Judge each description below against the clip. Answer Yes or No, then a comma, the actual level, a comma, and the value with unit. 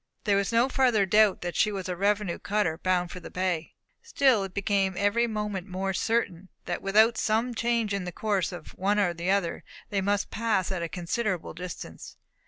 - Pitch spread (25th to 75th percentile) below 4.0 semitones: Yes, average, 2.9 semitones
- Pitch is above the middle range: Yes, high, 200 Hz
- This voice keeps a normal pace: Yes, average, 195 wpm